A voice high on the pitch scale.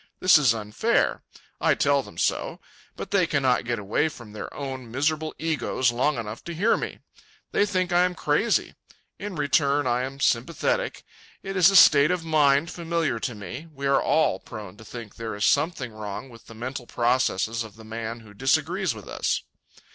No: low, 135 Hz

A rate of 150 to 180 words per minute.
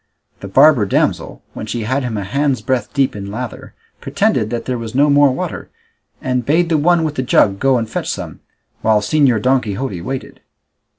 No: average, 195 wpm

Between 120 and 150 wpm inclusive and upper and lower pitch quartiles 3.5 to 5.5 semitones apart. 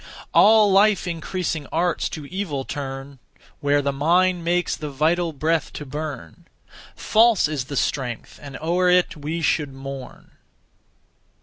Yes: slow, 135 wpm; average, 4.1 semitones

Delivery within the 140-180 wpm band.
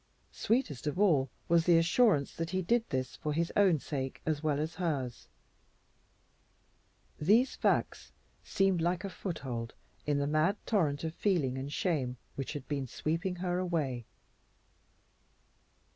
Yes: average, 145 wpm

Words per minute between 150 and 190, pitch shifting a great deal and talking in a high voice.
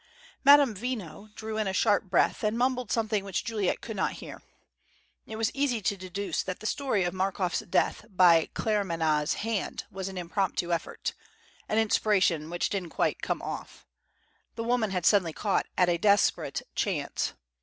No: average, 165 wpm; average, 3.5 semitones; high, 200 Hz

